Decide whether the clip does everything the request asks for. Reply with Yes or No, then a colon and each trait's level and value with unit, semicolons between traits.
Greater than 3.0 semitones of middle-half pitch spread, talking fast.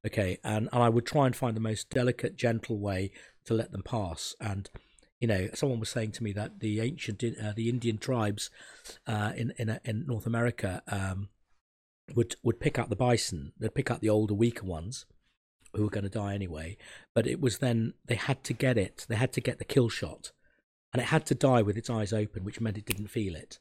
No: average, 2.7 semitones; fast, 230 wpm